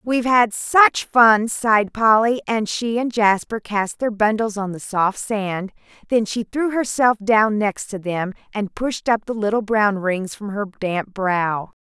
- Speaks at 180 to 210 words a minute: Yes, average, 185 wpm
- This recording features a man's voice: No, female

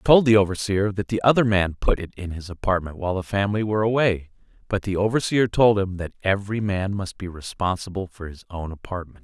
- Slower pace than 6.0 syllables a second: No, 6.1 syllables/s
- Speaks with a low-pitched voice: Yes, low, 100 Hz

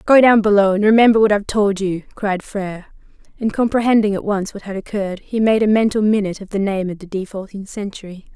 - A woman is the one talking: Yes, female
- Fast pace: Yes, fast, 215 wpm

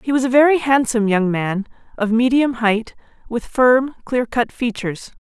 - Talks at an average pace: Yes, average, 160 wpm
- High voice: Yes, high, 240 Hz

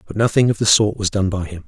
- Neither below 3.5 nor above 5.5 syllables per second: No, 6.6 syllables/s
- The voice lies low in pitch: Yes, low, 100 Hz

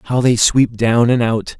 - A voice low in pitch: Yes, low, 115 Hz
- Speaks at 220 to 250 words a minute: Yes, fast, 225 wpm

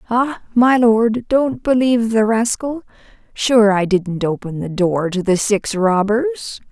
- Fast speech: No, average, 150 wpm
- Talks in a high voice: Yes, high, 220 Hz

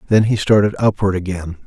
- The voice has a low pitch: Yes, low, 100 Hz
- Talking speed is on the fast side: No, average, 180 wpm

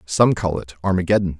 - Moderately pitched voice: No, very low, 90 Hz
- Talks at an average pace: Yes, average, 170 wpm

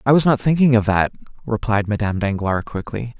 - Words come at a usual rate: Yes, average, 190 wpm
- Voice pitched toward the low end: Yes, low, 115 Hz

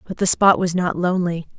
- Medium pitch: Yes, medium, 180 Hz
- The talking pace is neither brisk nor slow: No, fast, 230 wpm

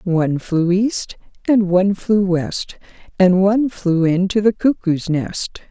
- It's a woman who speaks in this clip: Yes, female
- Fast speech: No, average, 145 wpm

